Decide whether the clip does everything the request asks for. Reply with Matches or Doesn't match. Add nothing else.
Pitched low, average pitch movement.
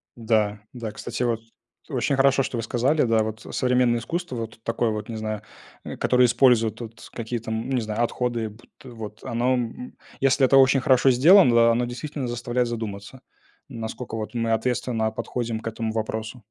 Doesn't match